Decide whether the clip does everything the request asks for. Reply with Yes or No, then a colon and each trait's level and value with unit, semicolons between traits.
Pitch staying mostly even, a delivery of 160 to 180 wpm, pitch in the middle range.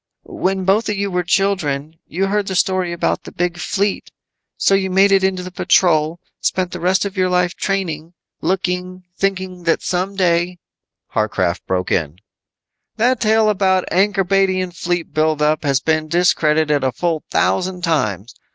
No: average, 3.3 semitones; average, 170 wpm; medium, 180 Hz